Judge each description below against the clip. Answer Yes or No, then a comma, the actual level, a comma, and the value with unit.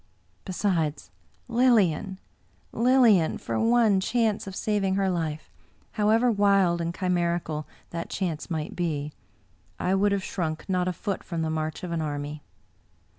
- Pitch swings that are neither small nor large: Yes, average, 4.2 semitones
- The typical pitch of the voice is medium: Yes, medium, 180 Hz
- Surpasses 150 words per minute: No, average, 145 wpm